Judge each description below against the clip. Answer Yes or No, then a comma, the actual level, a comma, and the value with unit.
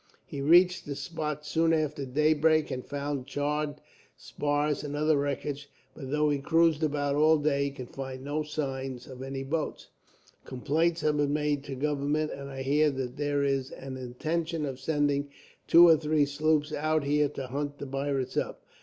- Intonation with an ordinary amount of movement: No, narrow, 1.8 semitones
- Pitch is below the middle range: No, medium, 145 Hz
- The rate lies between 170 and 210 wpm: Yes, average, 180 wpm